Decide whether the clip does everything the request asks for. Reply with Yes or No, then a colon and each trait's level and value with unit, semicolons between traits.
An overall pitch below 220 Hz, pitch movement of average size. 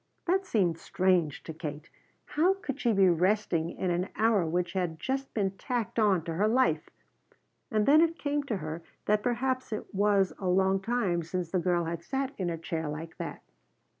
No: high, 190 Hz; wide, 5.8 semitones